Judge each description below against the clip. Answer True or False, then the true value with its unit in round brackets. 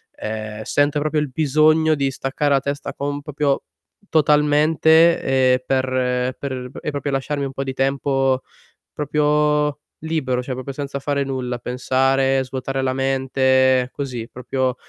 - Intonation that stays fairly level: True (2.1 semitones)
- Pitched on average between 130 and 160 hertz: True (135 Hz)